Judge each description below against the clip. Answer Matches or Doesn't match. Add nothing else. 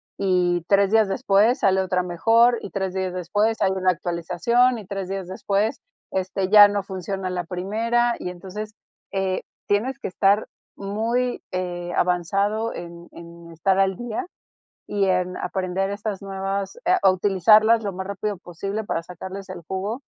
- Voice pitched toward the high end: Matches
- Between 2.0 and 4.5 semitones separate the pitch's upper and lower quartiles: Matches